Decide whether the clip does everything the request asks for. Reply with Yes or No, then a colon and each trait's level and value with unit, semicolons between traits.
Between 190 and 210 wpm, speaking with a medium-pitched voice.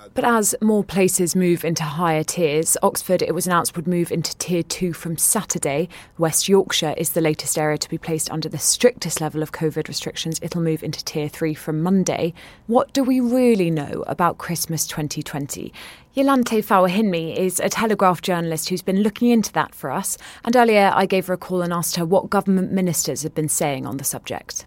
Yes: average, 200 wpm; medium, 170 Hz